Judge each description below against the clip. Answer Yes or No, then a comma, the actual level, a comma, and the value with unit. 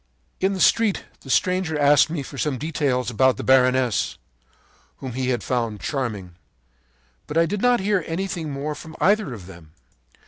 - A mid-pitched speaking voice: Yes, medium, 145 Hz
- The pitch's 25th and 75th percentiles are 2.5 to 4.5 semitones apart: No, average, 5.2 semitones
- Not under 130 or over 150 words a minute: No, average, 170 wpm